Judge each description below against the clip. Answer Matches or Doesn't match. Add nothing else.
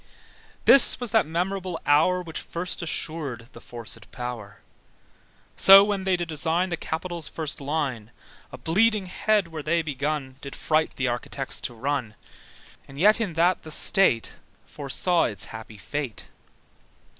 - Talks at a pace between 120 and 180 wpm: Matches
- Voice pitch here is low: Doesn't match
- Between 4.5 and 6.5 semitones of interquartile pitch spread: Matches